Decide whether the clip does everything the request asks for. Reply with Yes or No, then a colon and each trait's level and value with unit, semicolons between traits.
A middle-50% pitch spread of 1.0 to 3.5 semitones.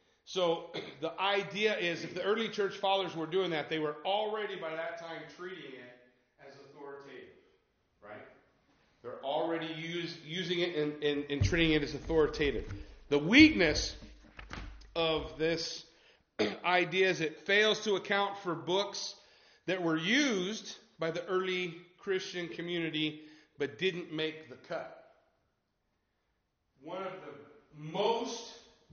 No: average, 4.0 semitones